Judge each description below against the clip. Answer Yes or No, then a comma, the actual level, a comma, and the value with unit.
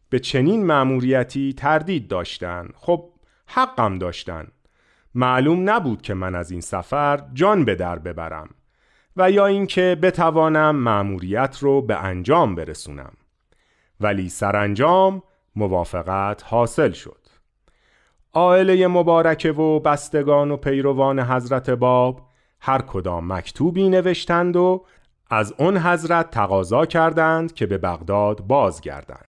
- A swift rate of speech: No, average, 115 wpm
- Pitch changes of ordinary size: No, wide, 8.6 semitones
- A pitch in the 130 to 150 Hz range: Yes, low, 135 Hz